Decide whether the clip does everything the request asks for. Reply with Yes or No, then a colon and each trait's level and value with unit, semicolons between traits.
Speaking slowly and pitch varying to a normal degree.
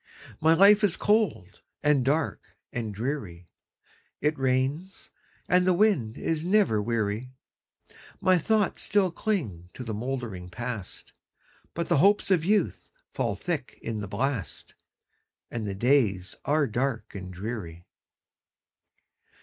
No: slow, 125 wpm; wide, 8.4 semitones